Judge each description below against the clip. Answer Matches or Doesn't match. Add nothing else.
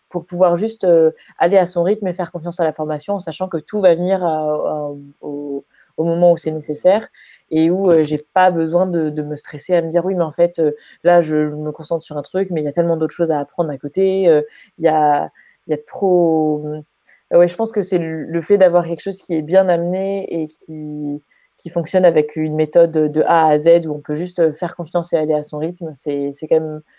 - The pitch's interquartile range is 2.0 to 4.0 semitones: Matches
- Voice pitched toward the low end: Doesn't match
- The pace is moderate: Doesn't match